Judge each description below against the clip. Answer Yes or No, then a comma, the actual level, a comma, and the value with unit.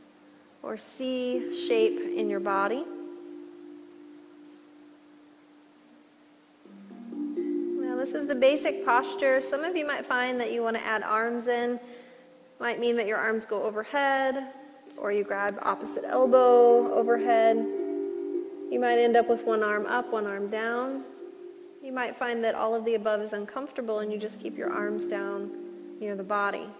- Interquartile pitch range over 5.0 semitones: Yes, wide, 5.6 semitones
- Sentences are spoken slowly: No, average, 150 wpm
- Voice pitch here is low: No, very high, 260 Hz